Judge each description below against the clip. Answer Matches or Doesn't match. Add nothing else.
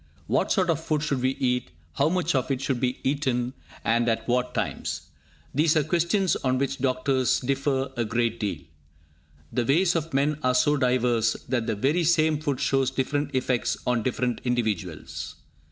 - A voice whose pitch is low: Matches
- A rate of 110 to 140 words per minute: Doesn't match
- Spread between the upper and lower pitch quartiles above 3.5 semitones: Doesn't match